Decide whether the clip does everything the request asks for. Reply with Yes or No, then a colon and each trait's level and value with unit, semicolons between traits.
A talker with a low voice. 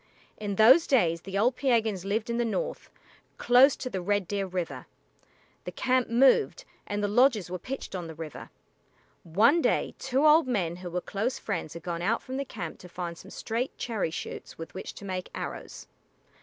No: high, 205 Hz